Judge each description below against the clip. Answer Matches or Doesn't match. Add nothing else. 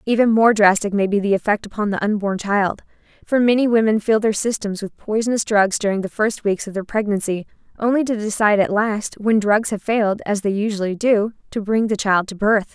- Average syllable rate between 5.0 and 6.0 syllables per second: Matches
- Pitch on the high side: Matches